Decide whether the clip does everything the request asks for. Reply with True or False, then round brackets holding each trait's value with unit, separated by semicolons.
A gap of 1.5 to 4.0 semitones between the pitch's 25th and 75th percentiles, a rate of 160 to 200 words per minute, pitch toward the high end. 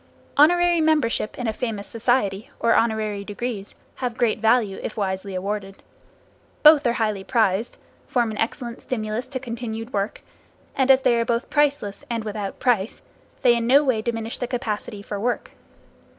True (3.1 semitones; 165 wpm; 230 Hz)